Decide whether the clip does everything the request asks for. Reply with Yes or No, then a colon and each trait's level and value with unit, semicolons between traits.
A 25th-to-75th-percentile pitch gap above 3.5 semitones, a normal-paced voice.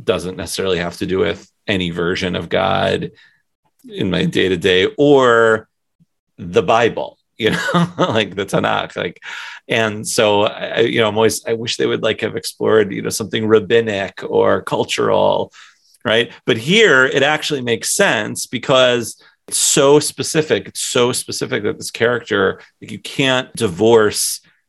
Yes: average, 3.9 semitones; average, 160 wpm